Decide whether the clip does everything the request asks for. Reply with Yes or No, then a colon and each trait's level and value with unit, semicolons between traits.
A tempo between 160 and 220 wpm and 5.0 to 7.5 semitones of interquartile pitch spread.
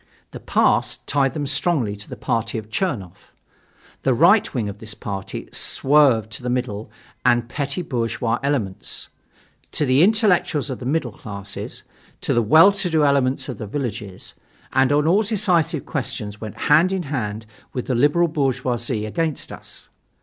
Yes: average, 165 wpm; wide, 5.6 semitones